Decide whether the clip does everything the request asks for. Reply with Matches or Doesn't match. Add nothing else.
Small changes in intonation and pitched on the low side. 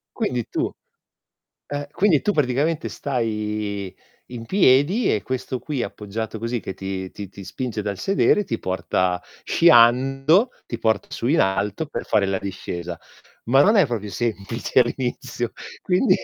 Doesn't match